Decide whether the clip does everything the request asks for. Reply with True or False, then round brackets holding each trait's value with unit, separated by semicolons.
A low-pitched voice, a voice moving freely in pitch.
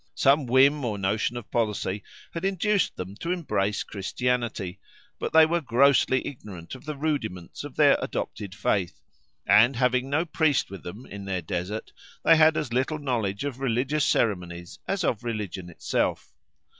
True (120 Hz; 6.4 semitones)